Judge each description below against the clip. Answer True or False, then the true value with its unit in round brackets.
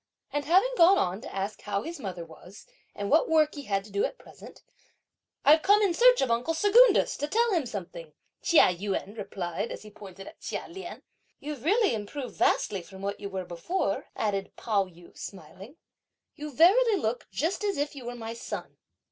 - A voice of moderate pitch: False (240 Hz)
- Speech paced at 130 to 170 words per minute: False (195 wpm)